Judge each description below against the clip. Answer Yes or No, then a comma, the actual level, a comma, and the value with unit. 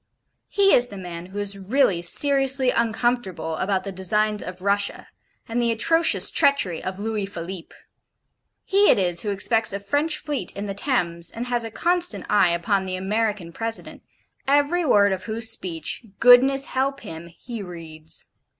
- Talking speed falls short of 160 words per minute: No, average, 165 wpm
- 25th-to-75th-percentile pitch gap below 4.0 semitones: No, average, 5.1 semitones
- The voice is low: No, high, 210 Hz